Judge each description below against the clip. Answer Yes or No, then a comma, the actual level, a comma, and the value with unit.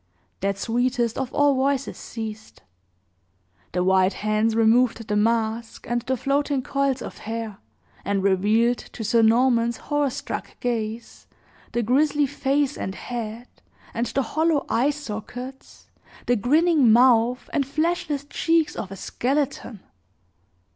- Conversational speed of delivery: No, slow, 130 wpm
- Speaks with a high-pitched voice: Yes, high, 240 Hz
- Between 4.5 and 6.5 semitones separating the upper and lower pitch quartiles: No, average, 3.9 semitones